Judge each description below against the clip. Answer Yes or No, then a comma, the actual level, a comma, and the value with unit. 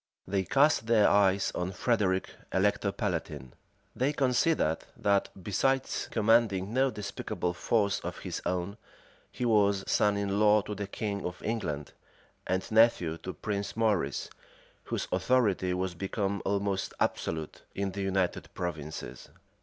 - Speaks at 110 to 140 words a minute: Yes, slow, 135 wpm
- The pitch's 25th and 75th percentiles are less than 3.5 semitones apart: Yes, average, 2.8 semitones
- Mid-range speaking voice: No, low, 100 Hz